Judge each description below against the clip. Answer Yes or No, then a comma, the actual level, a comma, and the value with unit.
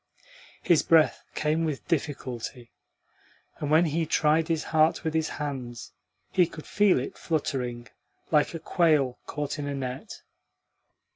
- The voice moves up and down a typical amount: Yes, average, 3.1 semitones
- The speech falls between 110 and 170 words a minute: Yes, average, 140 wpm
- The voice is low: No, medium, 150 Hz